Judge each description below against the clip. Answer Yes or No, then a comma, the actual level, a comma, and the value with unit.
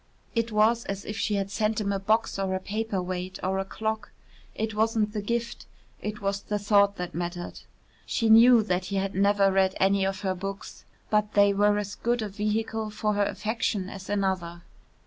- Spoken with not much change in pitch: Yes, narrow, 2.0 semitones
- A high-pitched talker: Yes, high, 205 Hz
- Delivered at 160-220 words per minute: Yes, average, 200 wpm